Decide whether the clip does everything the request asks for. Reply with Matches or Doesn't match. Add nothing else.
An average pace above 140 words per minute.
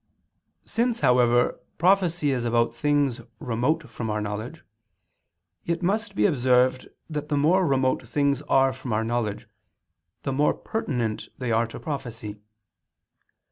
Doesn't match